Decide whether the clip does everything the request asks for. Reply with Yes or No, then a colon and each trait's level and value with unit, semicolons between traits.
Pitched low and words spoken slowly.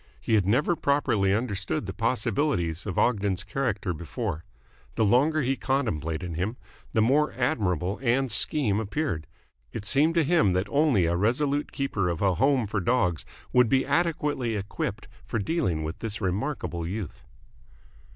No: low, 110 Hz; average, 150 wpm